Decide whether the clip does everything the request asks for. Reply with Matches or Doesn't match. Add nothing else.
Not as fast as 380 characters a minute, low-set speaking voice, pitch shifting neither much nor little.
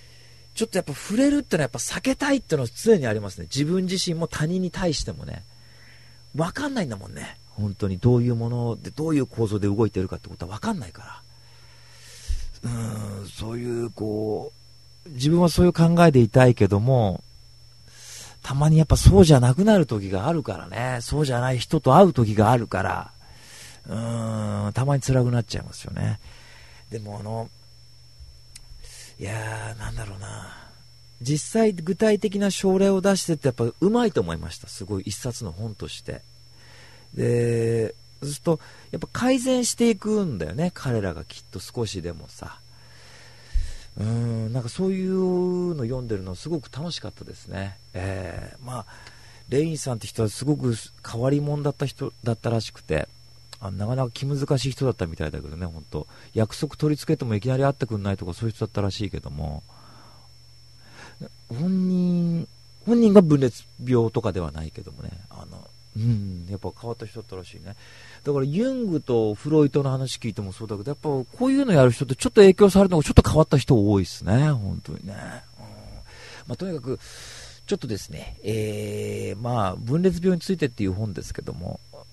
Doesn't match